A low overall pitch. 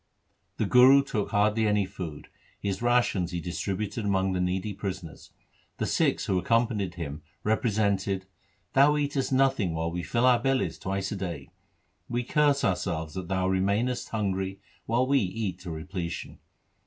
Yes: low, 100 Hz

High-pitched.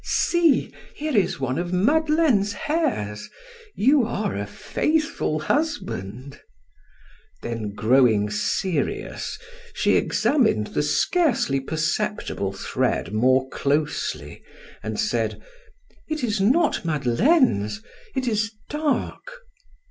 Yes: high, 200 Hz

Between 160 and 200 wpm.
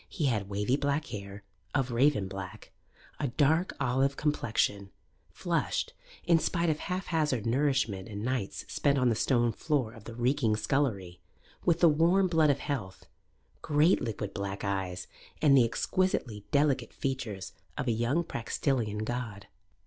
No: average, 150 wpm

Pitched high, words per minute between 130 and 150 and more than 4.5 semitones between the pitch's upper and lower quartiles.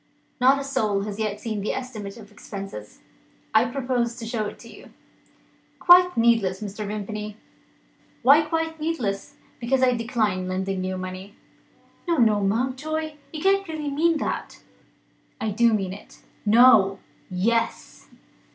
Yes: high, 225 Hz; average, 145 wpm; average, 5.1 semitones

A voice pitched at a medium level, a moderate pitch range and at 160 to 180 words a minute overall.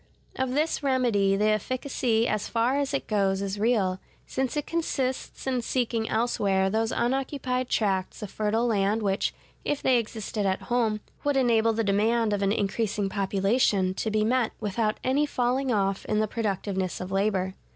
No: high, 220 Hz; average, 4.1 semitones; average, 170 wpm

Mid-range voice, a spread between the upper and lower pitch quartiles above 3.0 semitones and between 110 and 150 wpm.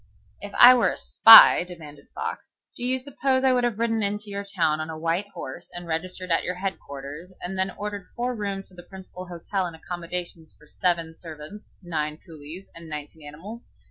No: medium, 180 Hz; average, 4.1 semitones; average, 200 wpm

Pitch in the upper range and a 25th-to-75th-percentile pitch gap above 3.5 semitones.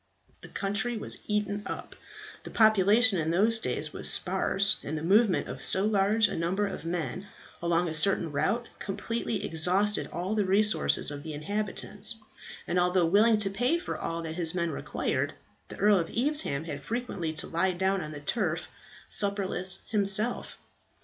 Yes: high, 195 Hz; average, 4.0 semitones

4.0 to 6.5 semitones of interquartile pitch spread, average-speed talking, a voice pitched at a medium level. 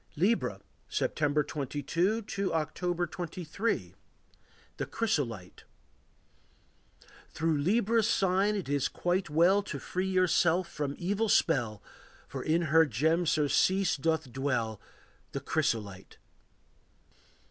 No: average, 4.7 semitones; slow, 105 wpm; medium, 165 Hz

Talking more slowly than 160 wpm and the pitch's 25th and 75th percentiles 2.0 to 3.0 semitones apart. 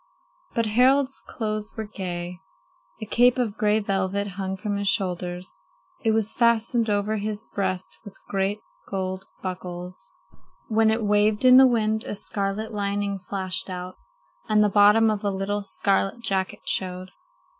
Yes: average, 150 wpm; narrow, 2.4 semitones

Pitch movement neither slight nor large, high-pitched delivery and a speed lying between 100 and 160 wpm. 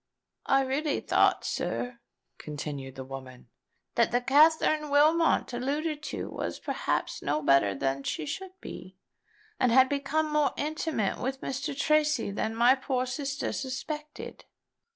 No: wide, 6.9 semitones; very high, 270 Hz; slow, 135 wpm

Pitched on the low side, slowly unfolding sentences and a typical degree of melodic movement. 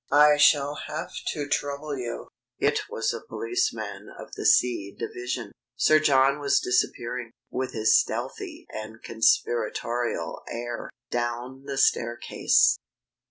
Yes: low, 120 Hz; slow, 125 wpm; average, 3.3 semitones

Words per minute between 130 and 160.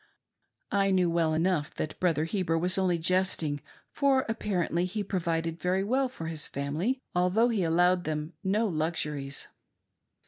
Yes: average, 150 wpm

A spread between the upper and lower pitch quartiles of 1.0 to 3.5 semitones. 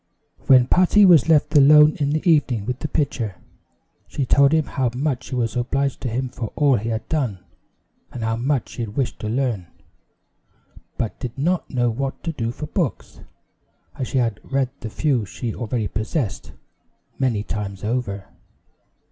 No: average, 4.1 semitones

